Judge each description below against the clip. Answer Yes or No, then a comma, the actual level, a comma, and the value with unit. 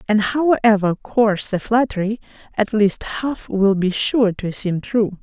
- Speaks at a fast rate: No, average, 160 wpm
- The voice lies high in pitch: Yes, high, 210 Hz